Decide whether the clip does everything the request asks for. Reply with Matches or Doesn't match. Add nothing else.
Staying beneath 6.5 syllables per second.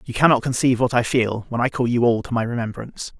Doesn't match